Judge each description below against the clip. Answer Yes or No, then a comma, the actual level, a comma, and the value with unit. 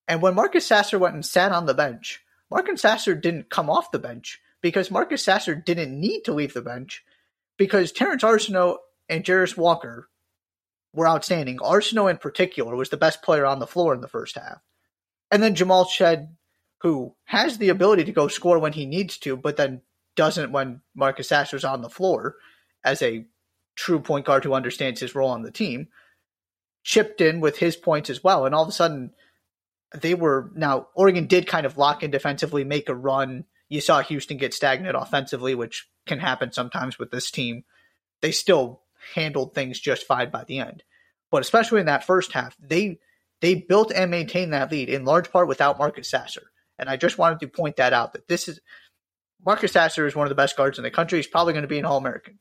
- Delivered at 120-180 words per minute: No, fast, 205 wpm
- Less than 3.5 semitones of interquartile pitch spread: No, average, 5.0 semitones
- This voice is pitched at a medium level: Yes, medium, 155 Hz